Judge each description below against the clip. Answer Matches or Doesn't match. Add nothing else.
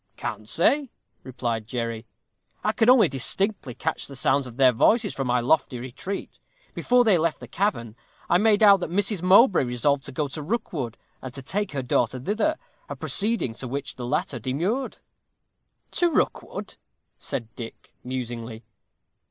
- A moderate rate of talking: Matches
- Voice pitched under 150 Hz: Matches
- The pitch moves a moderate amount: Doesn't match